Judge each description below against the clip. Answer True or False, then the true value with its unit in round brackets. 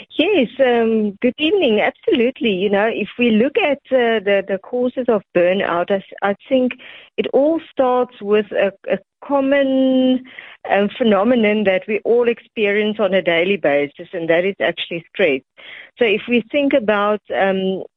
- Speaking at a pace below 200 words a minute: True (160 wpm)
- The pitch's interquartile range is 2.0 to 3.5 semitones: False (4.7 semitones)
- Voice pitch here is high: True (215 Hz)